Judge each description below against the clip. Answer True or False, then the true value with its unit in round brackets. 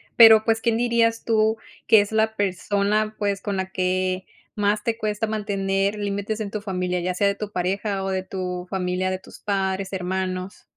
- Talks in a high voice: True (200 Hz)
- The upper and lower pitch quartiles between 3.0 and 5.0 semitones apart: False (2.4 semitones)